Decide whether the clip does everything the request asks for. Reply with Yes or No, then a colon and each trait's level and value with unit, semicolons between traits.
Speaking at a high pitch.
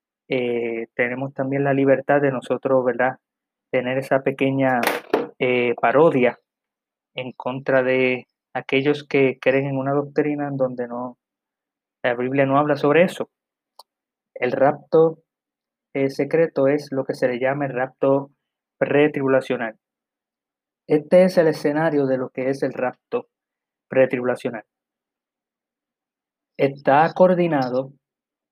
No: low, 135 Hz